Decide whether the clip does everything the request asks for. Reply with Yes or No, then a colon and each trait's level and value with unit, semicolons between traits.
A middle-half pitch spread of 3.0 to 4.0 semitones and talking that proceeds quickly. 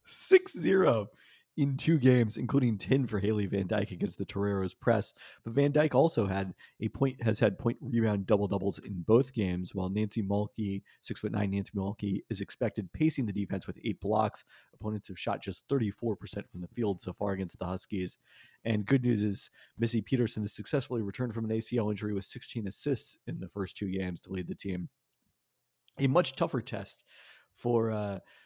No: average, 3.3 semitones; average, 190 wpm